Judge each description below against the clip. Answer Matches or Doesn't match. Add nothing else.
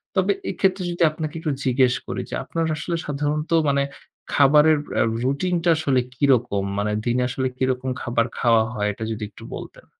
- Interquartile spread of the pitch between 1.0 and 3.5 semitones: Doesn't match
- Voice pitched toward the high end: Doesn't match